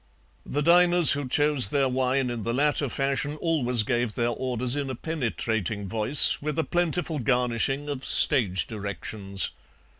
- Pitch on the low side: Yes, low, 130 Hz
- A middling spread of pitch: Yes, average, 4.0 semitones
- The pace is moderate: Yes, average, 150 wpm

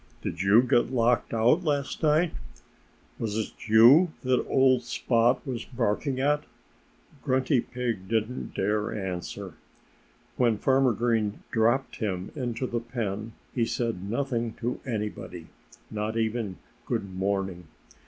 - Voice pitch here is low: Yes, low, 115 Hz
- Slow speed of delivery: Yes, slow, 125 wpm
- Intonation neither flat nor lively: Yes, average, 3.3 semitones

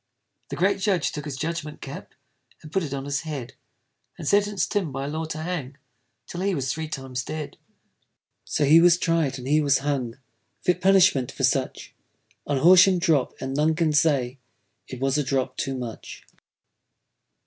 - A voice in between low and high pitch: Yes, medium, 150 Hz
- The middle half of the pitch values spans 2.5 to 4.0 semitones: Yes, average, 3.7 semitones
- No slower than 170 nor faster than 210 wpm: Yes, average, 175 wpm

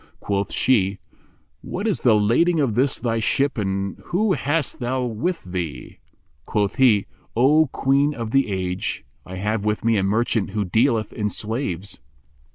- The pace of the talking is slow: No, average, 160 wpm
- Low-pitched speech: Yes, low, 115 Hz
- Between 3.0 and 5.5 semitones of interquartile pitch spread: Yes, average, 5.2 semitones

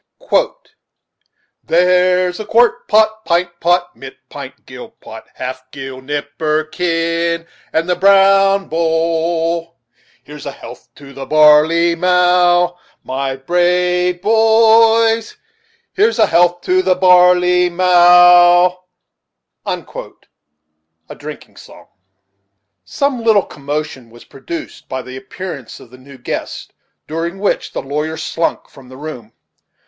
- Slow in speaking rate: Yes, slow, 110 wpm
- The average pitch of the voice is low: No, medium, 175 Hz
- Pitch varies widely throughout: No, average, 3.4 semitones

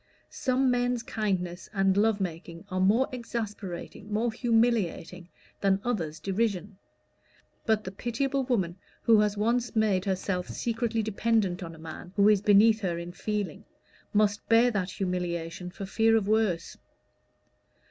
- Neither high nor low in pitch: No, high, 205 Hz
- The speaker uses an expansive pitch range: No, average, 3.7 semitones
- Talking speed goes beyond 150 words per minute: No, average, 140 wpm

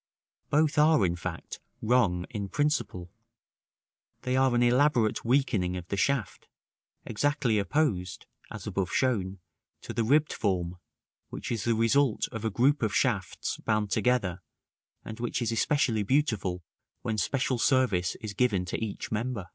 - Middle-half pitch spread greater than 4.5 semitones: Yes, average, 5.0 semitones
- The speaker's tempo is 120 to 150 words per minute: Yes, average, 145 wpm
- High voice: No, low, 115 Hz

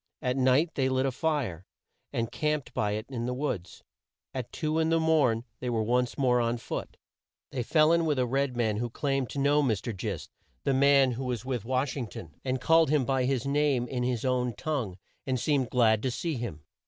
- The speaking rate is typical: No, fast, 215 wpm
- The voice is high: No, low, 130 Hz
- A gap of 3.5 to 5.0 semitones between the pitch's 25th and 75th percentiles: No, average, 2.9 semitones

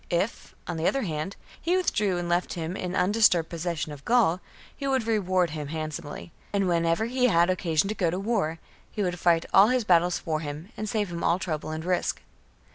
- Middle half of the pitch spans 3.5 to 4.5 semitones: Yes, average, 4.0 semitones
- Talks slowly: No, fast, 205 wpm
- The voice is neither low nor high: Yes, medium, 175 Hz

